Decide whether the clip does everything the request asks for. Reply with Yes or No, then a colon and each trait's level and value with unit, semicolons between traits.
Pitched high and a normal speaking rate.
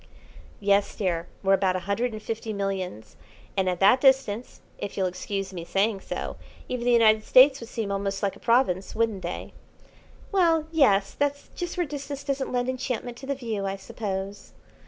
Yes: high, 215 Hz; average, 180 wpm